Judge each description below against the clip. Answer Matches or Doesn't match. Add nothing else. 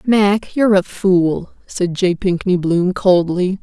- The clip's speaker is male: Doesn't match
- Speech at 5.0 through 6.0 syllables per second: Doesn't match